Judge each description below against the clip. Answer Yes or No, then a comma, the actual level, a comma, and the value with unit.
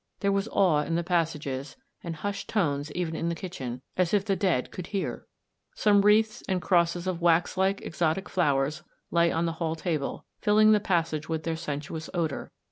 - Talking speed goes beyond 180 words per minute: Yes, average, 195 wpm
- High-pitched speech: No, medium, 170 Hz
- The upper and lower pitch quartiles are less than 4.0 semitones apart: Yes, average, 3.3 semitones